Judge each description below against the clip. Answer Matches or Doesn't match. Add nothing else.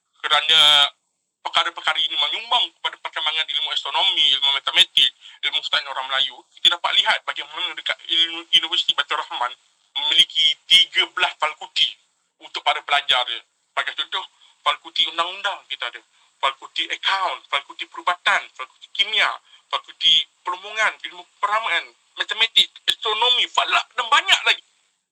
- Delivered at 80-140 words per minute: Matches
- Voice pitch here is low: Doesn't match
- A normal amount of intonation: Doesn't match